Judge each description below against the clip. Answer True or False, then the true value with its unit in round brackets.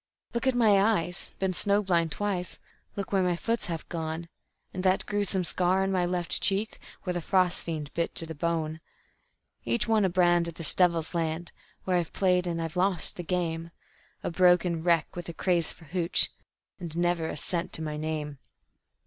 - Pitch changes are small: True (2.2 semitones)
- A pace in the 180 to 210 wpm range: True (190 wpm)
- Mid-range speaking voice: True (175 Hz)